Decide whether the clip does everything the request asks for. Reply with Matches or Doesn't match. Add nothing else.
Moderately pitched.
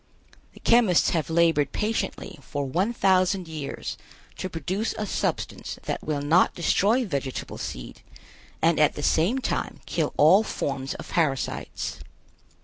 Matches